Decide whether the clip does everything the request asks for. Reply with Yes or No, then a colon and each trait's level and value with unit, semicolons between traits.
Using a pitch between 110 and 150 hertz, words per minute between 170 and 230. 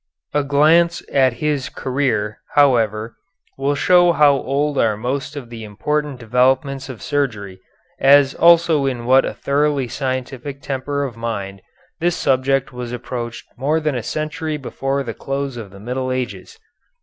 No: low, 135 Hz; average, 150 wpm